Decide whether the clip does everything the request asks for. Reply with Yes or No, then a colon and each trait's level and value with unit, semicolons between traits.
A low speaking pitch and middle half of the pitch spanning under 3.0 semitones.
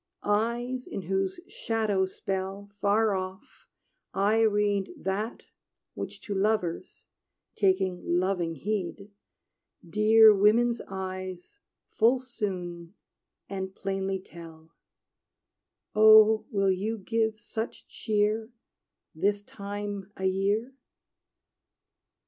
No: high, 200 Hz; narrow, 2.4 semitones